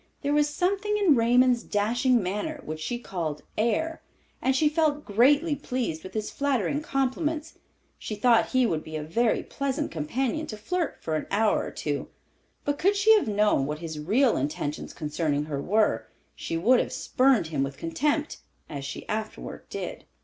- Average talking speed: Yes, average, 175 wpm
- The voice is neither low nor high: No, high, 235 Hz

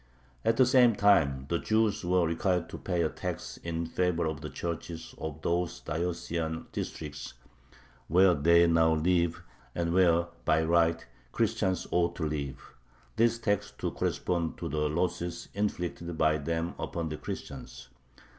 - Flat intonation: Yes, narrow, 2.1 semitones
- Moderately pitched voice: No, very low, 85 Hz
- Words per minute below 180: Yes, average, 150 wpm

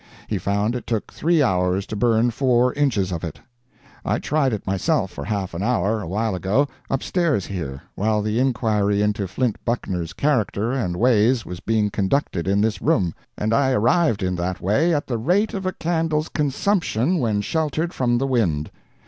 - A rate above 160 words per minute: Yes, average, 180 wpm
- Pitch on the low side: Yes, low, 110 Hz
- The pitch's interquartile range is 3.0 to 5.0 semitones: No, wide, 5.6 semitones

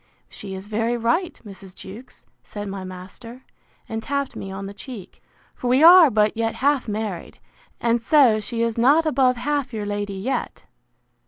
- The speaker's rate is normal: Yes, average, 170 wpm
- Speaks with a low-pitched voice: No, high, 230 Hz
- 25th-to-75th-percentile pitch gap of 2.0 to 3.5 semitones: No, average, 4.0 semitones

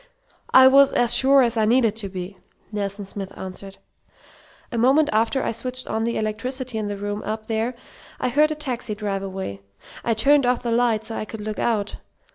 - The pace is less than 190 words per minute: No, average, 200 wpm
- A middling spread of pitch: Yes, average, 3.5 semitones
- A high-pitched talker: Yes, high, 225 Hz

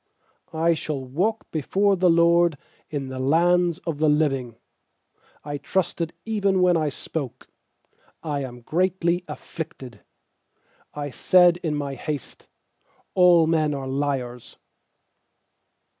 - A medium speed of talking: No, slow, 115 wpm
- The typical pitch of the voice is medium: Yes, medium, 155 Hz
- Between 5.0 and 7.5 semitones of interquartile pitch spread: No, average, 4.0 semitones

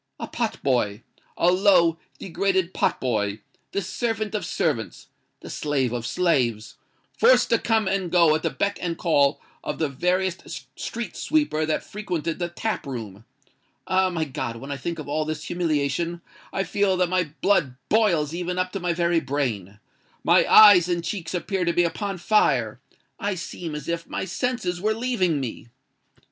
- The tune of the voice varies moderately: Yes, average, 4.7 semitones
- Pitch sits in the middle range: Yes, medium, 170 Hz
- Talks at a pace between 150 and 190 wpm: Yes, average, 160 wpm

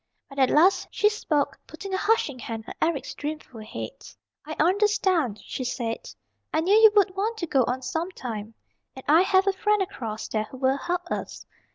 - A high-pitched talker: Yes, very high, 315 Hz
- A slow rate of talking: No, average, 190 wpm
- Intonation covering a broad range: Yes, wide, 6.8 semitones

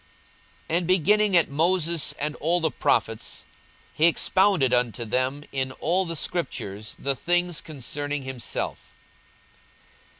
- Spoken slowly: Yes, slow, 125 wpm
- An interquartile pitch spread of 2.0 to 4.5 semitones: No, average, 4.9 semitones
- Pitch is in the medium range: Yes, medium, 155 Hz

